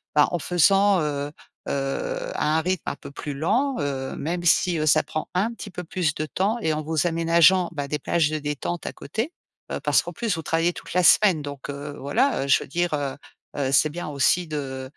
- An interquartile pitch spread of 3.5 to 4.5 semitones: Yes, average, 3.9 semitones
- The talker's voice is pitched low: No, medium, 160 Hz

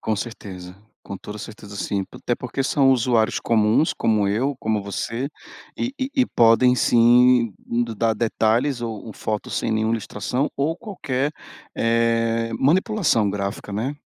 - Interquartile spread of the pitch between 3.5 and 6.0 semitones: No, average, 3.1 semitones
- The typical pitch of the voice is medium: No, low, 115 Hz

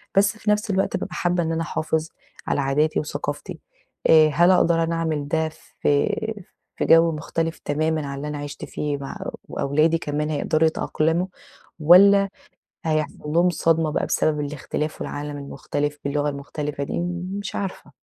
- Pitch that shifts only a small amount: Yes, narrow, 2.3 semitones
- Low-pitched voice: No, medium, 155 Hz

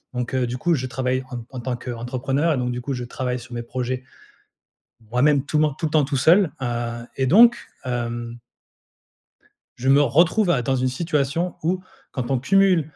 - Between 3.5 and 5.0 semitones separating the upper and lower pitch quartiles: Yes, average, 3.8 semitones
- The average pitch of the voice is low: Yes, low, 130 Hz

